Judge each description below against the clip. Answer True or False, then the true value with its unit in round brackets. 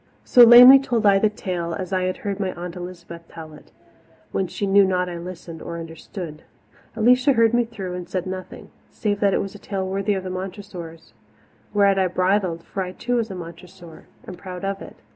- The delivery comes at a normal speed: False (210 wpm)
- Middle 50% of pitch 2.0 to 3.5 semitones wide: True (2.6 semitones)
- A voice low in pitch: False (190 Hz)